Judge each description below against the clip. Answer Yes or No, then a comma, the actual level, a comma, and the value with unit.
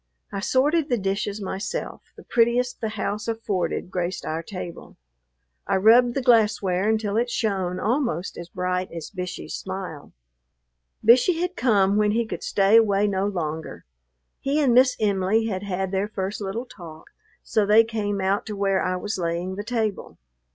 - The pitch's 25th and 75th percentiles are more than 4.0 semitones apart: No, average, 3.3 semitones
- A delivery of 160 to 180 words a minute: Yes, average, 165 wpm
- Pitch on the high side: Yes, high, 205 Hz